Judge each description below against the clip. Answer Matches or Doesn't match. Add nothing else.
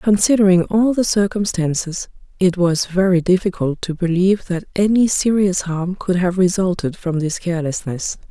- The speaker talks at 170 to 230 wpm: Doesn't match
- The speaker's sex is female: Matches